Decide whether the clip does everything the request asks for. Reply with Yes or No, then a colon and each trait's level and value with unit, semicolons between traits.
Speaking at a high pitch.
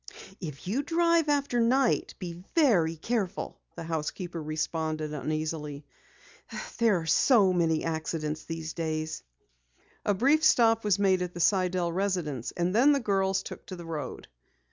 No: medium, 180 Hz